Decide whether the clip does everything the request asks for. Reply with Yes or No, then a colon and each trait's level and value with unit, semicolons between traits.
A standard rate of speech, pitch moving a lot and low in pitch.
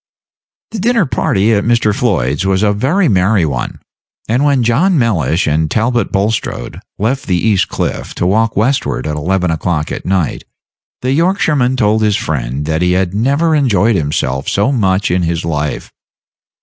Yes: average, 165 wpm; wide, 6.5 semitones; low, 100 Hz